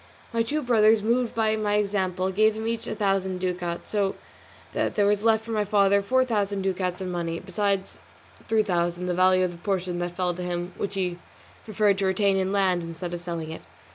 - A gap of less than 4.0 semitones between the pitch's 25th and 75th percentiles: Yes, average, 2.9 semitones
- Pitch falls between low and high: No, high, 195 Hz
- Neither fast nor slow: No, fast, 210 wpm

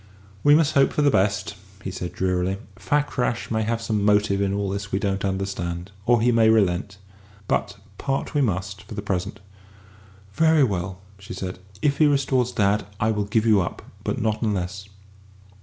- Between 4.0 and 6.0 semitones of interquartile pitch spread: No, average, 3.2 semitones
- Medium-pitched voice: No, low, 105 Hz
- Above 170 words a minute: Yes, average, 180 wpm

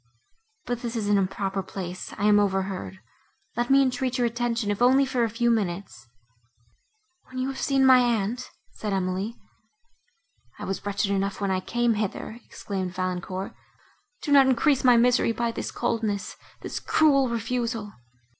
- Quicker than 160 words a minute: No, average, 150 wpm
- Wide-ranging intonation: No, average, 4.3 semitones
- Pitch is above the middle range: Yes, high, 225 Hz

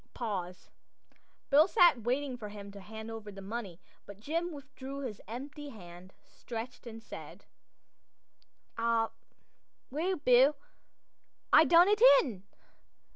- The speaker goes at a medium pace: No, slow, 125 wpm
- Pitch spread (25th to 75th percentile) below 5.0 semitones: No, wide, 5.5 semitones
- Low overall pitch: No, high, 235 Hz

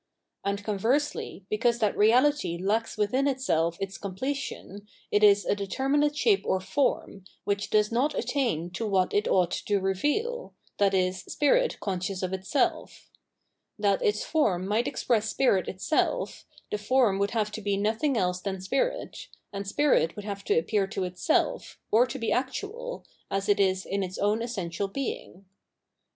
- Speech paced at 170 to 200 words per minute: No, average, 160 wpm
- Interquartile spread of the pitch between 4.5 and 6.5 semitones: Yes, average, 5.2 semitones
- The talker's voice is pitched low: No, high, 205 Hz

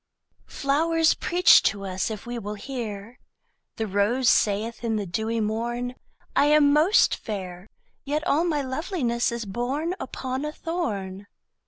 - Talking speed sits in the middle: Yes, average, 145 wpm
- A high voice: Yes, high, 240 Hz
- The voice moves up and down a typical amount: No, wide, 5.8 semitones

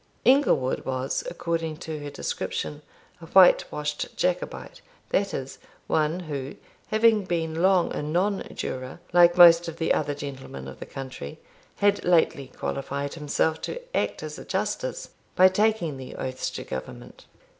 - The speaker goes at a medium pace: Yes, average, 150 wpm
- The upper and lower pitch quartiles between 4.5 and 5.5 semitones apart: Yes, average, 4.9 semitones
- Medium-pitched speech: Yes, medium, 160 Hz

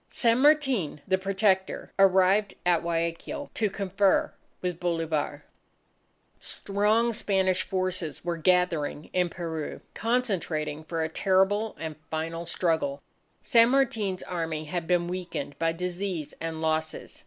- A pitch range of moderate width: Yes, average, 3.3 semitones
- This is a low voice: No, medium, 180 Hz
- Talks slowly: Yes, slow, 120 wpm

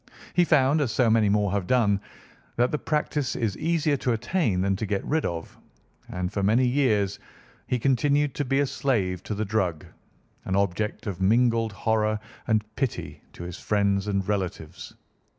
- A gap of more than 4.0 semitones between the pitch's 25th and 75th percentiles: Yes, average, 4.8 semitones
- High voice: No, low, 110 Hz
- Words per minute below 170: No, average, 175 wpm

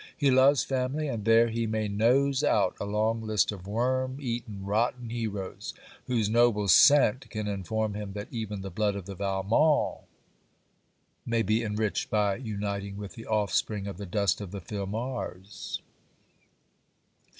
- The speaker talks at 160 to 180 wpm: No, average, 150 wpm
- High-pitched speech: No, low, 110 Hz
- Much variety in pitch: No, average, 2.9 semitones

